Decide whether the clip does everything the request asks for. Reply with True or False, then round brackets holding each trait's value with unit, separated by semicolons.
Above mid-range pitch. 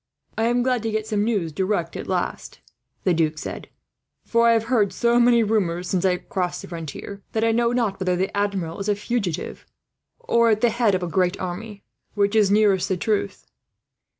True (205 Hz)